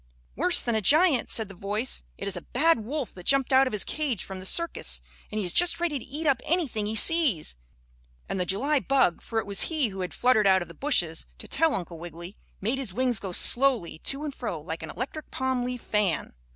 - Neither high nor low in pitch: No, high, 230 Hz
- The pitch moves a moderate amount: No, wide, 6.4 semitones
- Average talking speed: No, fast, 235 wpm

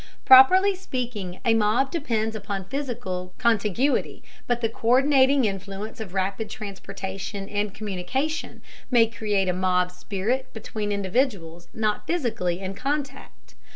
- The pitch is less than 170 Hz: No, high, 215 Hz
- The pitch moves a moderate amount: Yes, average, 5.0 semitones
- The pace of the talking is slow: Yes, slow, 120 wpm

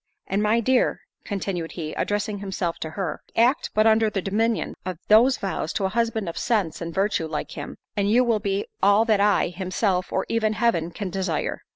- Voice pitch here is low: No, high, 200 Hz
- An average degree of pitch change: Yes, average, 3.3 semitones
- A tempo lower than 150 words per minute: No, average, 200 wpm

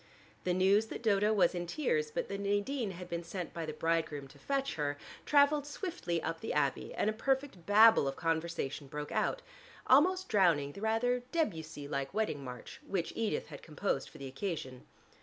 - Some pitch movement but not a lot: No, wide, 7.0 semitones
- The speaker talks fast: No, average, 185 wpm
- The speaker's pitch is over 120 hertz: Yes, medium, 185 Hz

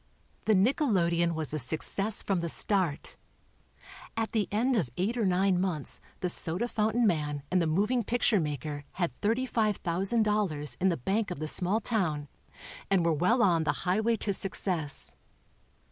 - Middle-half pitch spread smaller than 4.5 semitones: No, average, 5.0 semitones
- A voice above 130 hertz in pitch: Yes, medium, 185 Hz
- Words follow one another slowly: No, average, 160 wpm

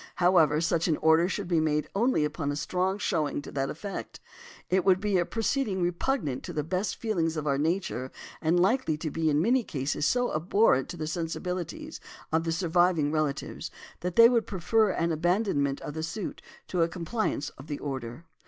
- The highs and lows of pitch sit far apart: No, average, 4.0 semitones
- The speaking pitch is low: No, medium, 170 Hz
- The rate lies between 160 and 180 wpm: No, average, 190 wpm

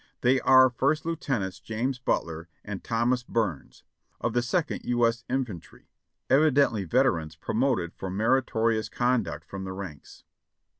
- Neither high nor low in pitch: No, low, 115 Hz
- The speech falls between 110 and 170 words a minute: Yes, average, 140 wpm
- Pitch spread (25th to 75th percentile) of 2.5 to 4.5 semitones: No, average, 5.3 semitones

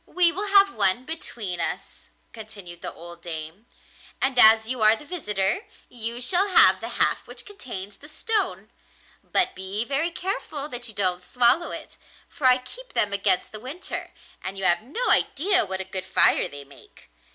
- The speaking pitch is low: No, high, 235 Hz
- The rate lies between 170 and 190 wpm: Yes, average, 180 wpm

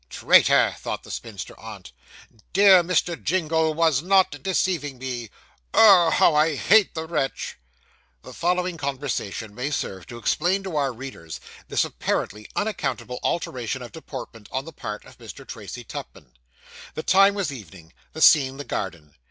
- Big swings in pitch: Yes, wide, 6.5 semitones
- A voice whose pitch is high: No, medium, 150 Hz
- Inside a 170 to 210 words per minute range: No, average, 150 wpm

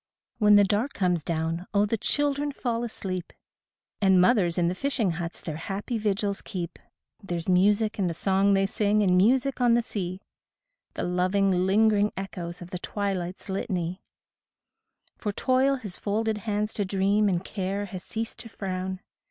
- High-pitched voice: Yes, high, 195 Hz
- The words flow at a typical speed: Yes, average, 170 wpm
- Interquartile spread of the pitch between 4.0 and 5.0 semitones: No, average, 2.8 semitones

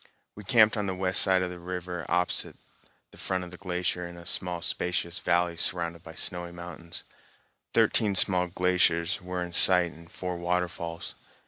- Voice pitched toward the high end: No, very low, 90 Hz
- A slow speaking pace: No, average, 165 wpm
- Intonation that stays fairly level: Yes, narrow, 1.1 semitones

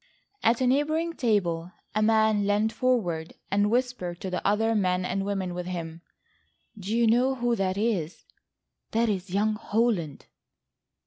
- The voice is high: Yes, high, 210 Hz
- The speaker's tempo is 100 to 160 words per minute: Yes, average, 145 wpm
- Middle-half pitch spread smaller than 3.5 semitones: No, average, 4.2 semitones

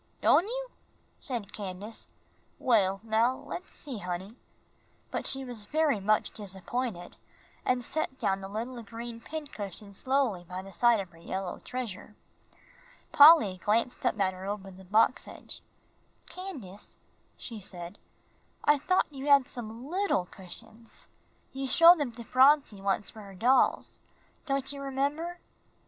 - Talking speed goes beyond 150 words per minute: No, average, 140 wpm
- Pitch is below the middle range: No, high, 230 Hz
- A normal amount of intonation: No, wide, 5.7 semitones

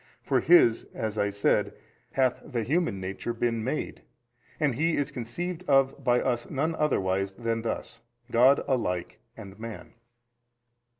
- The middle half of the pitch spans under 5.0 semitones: Yes, average, 4.2 semitones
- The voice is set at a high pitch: No, low, 120 Hz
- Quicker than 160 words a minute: No, average, 140 wpm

